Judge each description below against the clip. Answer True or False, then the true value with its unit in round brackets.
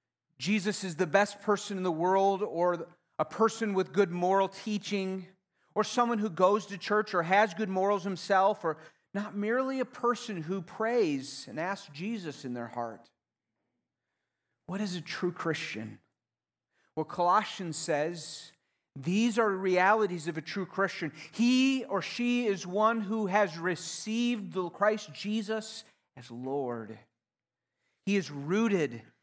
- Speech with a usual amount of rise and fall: True (4.6 semitones)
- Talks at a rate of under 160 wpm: True (145 wpm)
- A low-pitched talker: False (190 Hz)